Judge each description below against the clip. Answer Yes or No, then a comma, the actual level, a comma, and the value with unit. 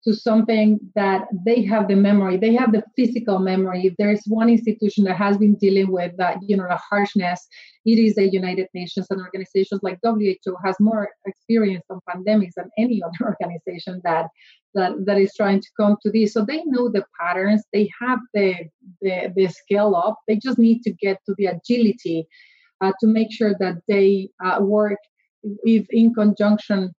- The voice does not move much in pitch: Yes, narrow, 2.3 semitones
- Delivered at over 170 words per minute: Yes, average, 190 wpm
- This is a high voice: Yes, high, 205 Hz